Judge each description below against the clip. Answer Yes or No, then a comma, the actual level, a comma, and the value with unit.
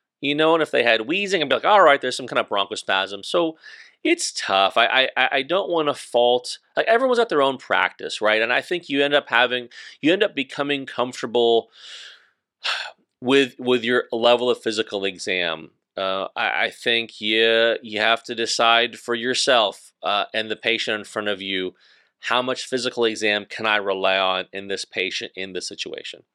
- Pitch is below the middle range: Yes, low, 120 Hz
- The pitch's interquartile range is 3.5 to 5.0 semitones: Yes, average, 4.4 semitones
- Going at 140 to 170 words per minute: No, average, 200 wpm